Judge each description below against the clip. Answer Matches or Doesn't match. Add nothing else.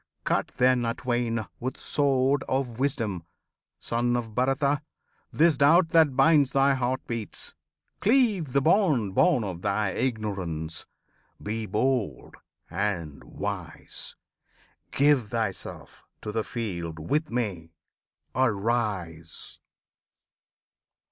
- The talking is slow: Matches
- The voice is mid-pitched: Doesn't match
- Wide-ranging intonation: Doesn't match